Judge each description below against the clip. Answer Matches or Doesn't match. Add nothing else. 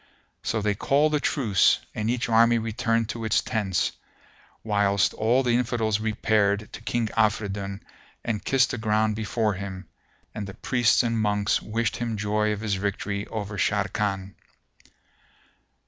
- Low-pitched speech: Matches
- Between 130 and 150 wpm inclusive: Matches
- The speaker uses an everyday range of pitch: Doesn't match